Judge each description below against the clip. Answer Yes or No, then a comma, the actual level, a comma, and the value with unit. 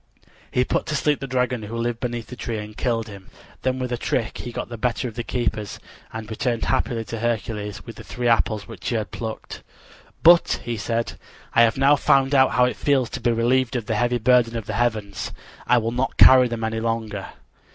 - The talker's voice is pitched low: Yes, low, 115 Hz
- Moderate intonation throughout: No, narrow, 2.1 semitones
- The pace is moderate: No, fast, 225 wpm